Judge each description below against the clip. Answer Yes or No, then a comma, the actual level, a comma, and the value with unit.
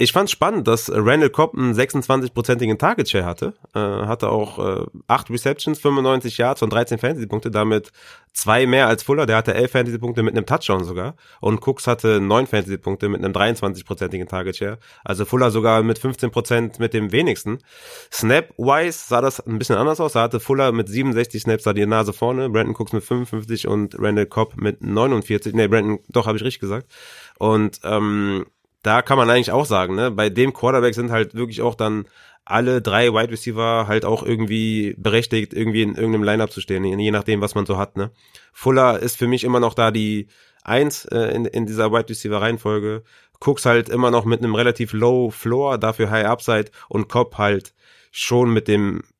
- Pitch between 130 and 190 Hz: No, low, 115 Hz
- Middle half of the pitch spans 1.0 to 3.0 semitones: Yes, narrow, 2.6 semitones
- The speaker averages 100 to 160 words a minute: No, fast, 190 wpm